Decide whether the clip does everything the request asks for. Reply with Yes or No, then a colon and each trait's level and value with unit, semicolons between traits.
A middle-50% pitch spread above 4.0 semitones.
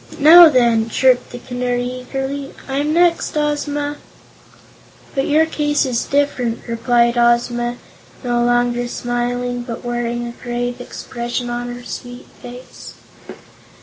No: narrow, 2.4 semitones